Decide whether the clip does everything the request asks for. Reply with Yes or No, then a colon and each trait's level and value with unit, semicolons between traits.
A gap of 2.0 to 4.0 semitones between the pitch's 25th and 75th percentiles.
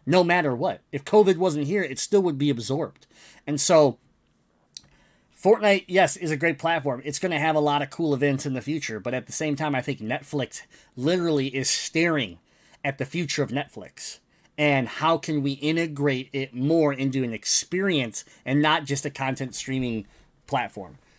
Yes: average, 3.4 semitones